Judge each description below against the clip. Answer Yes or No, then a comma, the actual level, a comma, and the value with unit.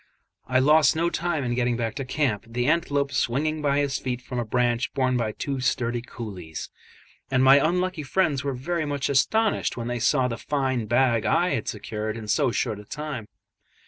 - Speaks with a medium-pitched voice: No, low, 130 Hz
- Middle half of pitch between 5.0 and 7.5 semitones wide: No, average, 3.5 semitones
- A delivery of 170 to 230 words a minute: Yes, average, 195 wpm